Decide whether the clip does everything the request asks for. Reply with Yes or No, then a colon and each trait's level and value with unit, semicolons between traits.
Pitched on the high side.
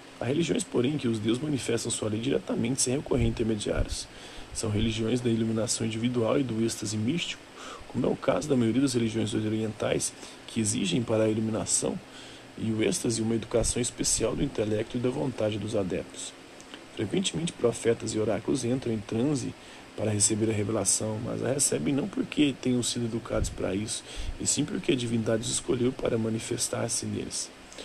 No: low, 115 Hz